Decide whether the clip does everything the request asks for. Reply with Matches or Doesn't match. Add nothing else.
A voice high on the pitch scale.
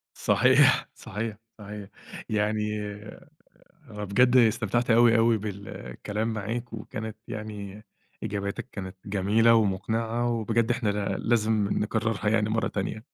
Doesn't match